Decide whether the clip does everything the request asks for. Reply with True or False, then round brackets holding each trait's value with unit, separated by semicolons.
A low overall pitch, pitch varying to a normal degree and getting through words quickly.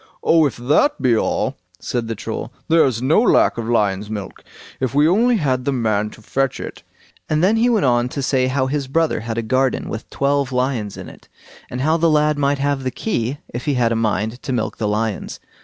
True (130 Hz; 4.3 semitones; 225 wpm)